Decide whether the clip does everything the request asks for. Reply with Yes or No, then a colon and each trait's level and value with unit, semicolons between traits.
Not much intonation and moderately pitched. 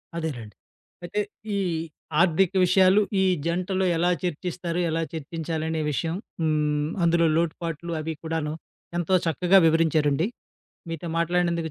Yes: narrow, 1.8 semitones; medium, 165 Hz